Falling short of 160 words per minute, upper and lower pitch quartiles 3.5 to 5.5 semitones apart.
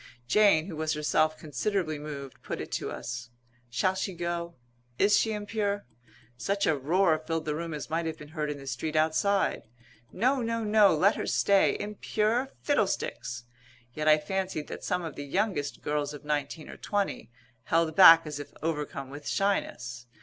No: average, 175 wpm; average, 5.0 semitones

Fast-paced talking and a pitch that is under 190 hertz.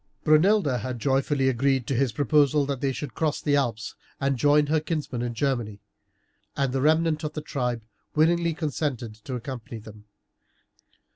No: average, 160 wpm; low, 135 Hz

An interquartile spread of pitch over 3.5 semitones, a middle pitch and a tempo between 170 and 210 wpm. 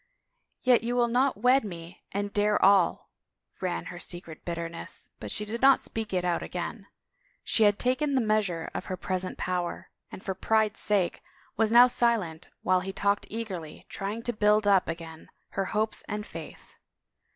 No: average, 3.9 semitones; high, 205 Hz; average, 175 wpm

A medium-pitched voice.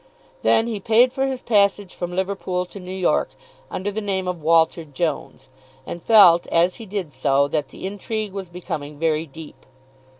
Yes: medium, 180 Hz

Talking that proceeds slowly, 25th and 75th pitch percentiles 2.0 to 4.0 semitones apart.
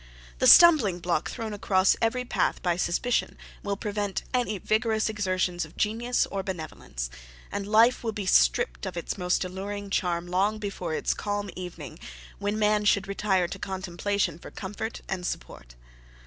No: average, 160 wpm; average, 3.0 semitones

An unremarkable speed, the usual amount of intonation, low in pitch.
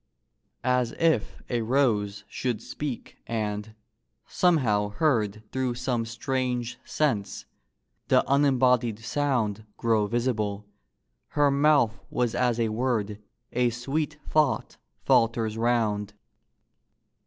No: slow, 100 wpm; average, 3.3 semitones; low, 120 Hz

